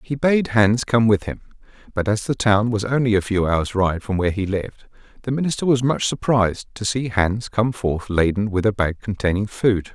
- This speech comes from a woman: No, male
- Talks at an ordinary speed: No, fast, 215 wpm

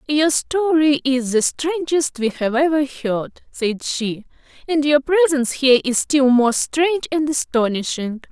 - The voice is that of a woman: Yes, female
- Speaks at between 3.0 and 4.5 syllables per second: Yes, 4.2 syllables/s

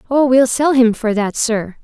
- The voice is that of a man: No, female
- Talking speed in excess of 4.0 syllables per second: Yes, 4.4 syllables/s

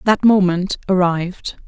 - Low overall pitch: No, medium, 185 Hz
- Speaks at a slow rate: Yes, slow, 105 wpm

